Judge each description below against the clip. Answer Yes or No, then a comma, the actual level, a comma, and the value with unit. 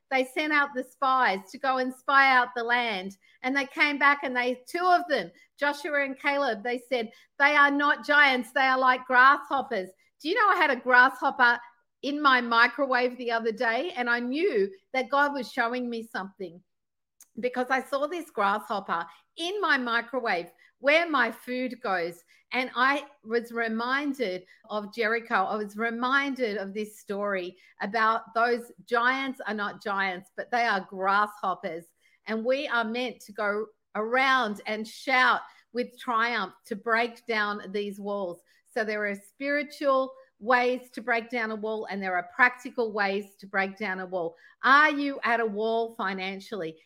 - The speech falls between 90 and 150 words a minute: No, average, 170 wpm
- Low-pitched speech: No, high, 240 Hz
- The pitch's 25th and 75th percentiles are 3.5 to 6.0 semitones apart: Yes, average, 4.1 semitones